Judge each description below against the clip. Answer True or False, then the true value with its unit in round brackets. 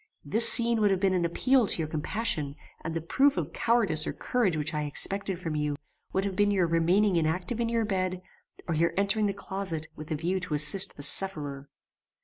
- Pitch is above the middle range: False (180 Hz)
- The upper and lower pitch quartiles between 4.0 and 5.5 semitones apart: True (4.4 semitones)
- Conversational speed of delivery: False (210 wpm)